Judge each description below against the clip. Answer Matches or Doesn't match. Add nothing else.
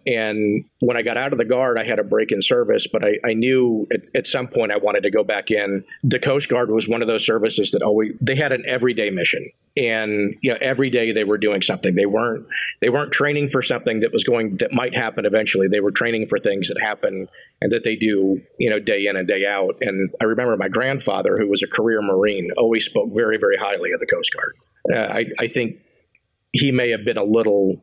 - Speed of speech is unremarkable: Doesn't match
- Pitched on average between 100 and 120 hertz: Matches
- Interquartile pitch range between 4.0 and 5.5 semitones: Matches